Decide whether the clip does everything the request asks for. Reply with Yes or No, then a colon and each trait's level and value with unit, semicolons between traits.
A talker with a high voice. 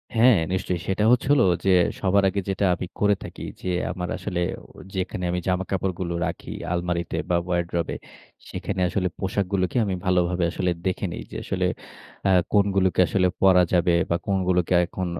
No: very low, 95 Hz